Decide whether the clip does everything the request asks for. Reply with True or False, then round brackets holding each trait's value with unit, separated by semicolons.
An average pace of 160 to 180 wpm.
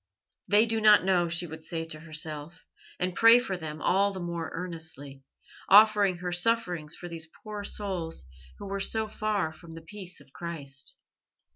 True (170 wpm)